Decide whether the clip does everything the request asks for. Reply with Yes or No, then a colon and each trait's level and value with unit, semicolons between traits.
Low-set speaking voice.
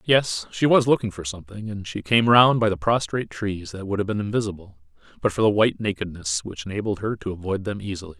Yes: low, 100 Hz